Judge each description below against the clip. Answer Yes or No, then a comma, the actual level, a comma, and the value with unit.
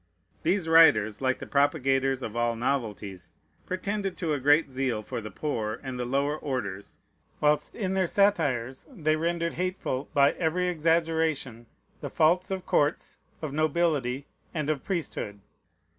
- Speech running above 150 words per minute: No, average, 145 wpm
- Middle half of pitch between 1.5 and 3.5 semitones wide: No, average, 4.6 semitones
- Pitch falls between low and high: Yes, medium, 145 Hz